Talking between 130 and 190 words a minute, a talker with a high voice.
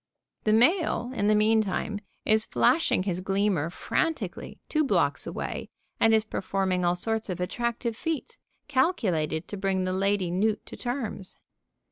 Yes: average, 145 wpm; high, 210 Hz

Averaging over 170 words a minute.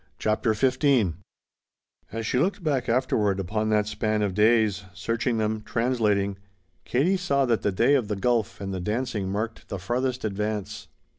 No: average, 160 wpm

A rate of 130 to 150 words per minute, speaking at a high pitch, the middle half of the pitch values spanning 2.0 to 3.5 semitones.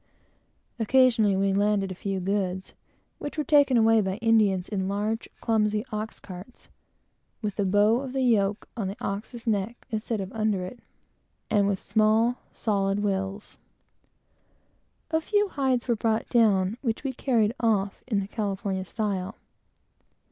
Yes: average, 140 wpm; high, 210 Hz; average, 2.8 semitones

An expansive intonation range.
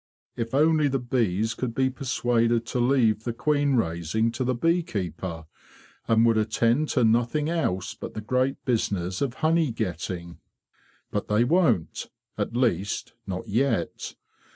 No: average, 4.1 semitones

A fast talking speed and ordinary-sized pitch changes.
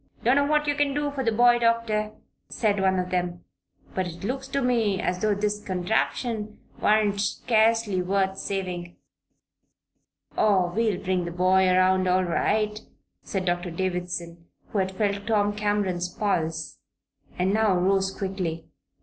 No: average, 150 wpm; average, 3.1 semitones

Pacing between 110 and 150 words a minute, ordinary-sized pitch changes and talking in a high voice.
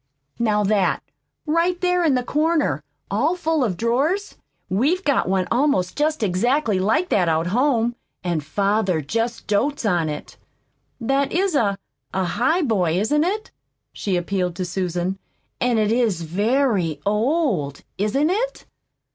No: average, 140 wpm; wide, 8.1 semitones; high, 225 Hz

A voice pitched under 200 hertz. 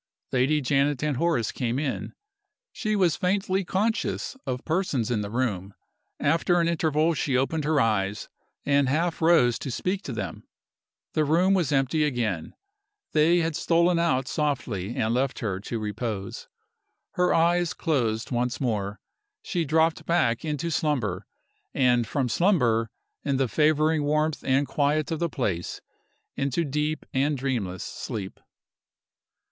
Yes: medium, 140 Hz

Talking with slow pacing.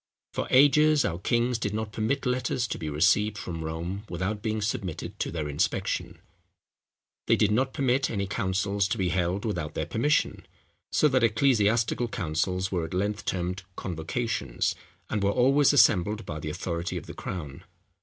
No: average, 165 wpm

